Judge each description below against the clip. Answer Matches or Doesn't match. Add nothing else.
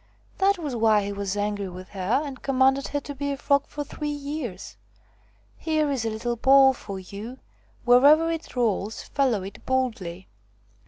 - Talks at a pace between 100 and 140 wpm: Doesn't match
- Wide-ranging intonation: Matches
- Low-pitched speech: Doesn't match